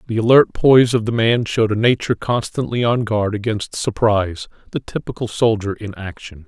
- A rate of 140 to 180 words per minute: Yes, average, 165 wpm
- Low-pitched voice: Yes, low, 110 Hz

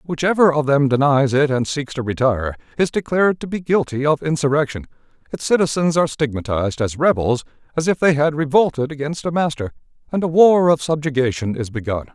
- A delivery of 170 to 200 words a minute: Yes, average, 185 wpm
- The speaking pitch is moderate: Yes, medium, 145 Hz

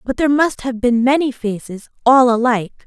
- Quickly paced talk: No, average, 170 wpm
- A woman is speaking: Yes, female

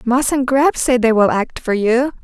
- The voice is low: No, very high, 250 Hz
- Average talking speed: No, fast, 240 wpm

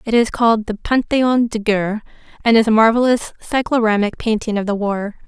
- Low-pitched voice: No, high, 225 Hz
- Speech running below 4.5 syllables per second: No, 5.5 syllables/s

